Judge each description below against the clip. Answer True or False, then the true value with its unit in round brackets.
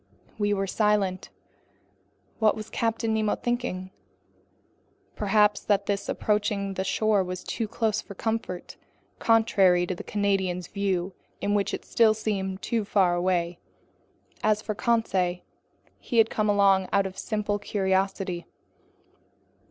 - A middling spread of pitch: False (2.3 semitones)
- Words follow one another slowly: True (130 wpm)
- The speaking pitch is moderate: False (200 Hz)